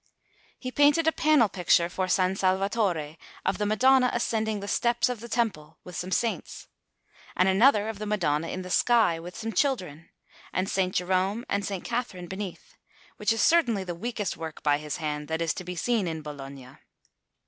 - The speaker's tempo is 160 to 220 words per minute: Yes, average, 185 wpm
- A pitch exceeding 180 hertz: Yes, high, 190 Hz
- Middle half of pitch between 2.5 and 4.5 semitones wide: No, average, 5.3 semitones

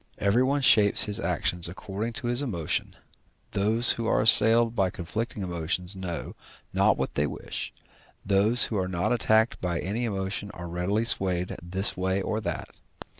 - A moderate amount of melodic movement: Yes, average, 3.8 semitones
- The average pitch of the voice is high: No, low, 100 Hz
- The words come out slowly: No, average, 160 wpm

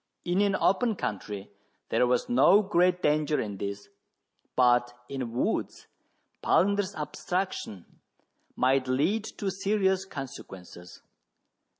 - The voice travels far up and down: Yes, wide, 7.9 semitones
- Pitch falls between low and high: Yes, medium, 150 Hz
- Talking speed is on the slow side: Yes, slow, 105 wpm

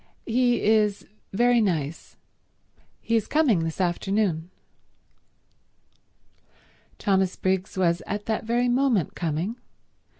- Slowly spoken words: Yes, slow, 100 wpm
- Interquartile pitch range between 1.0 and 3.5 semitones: No, average, 4.6 semitones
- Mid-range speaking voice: No, high, 205 Hz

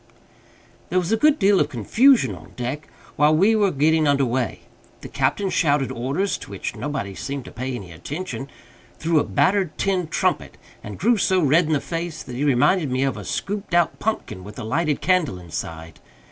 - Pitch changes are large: Yes, wide, 6.4 semitones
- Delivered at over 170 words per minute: Yes, average, 195 wpm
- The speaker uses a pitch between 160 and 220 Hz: No, medium, 150 Hz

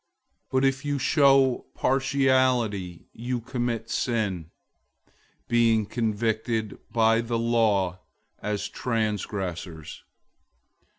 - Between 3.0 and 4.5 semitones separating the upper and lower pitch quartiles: Yes, average, 3.5 semitones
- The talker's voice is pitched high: No, low, 115 Hz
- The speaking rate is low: Yes, slow, 85 wpm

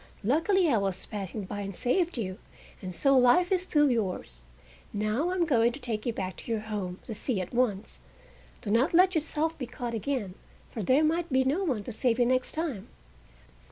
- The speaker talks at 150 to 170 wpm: No, fast, 205 wpm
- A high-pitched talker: Yes, high, 245 Hz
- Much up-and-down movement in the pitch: Yes, wide, 6.5 semitones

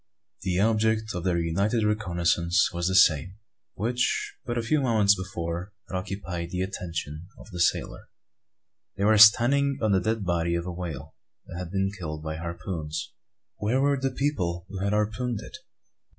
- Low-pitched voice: Yes, very low, 95 Hz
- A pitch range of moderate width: Yes, average, 4.2 semitones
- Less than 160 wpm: No, average, 170 wpm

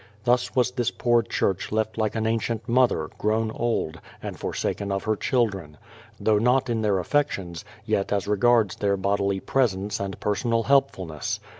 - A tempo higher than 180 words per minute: No, average, 165 wpm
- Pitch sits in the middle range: No, low, 110 Hz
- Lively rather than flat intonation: No, average, 3.2 semitones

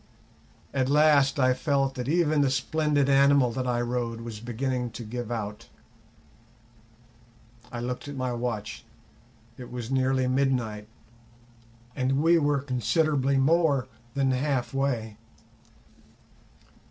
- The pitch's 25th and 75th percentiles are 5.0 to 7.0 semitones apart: No, narrow, 2.6 semitones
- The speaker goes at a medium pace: No, slow, 120 wpm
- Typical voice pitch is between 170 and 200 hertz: No, low, 130 Hz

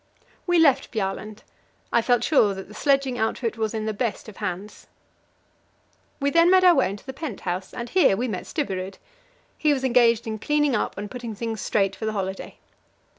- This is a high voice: Yes, high, 230 Hz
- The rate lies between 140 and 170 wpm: No, average, 195 wpm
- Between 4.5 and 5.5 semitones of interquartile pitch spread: Yes, average, 4.9 semitones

